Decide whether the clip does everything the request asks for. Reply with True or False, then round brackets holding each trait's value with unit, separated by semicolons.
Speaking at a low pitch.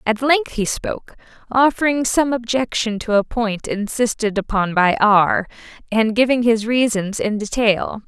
False (225 Hz)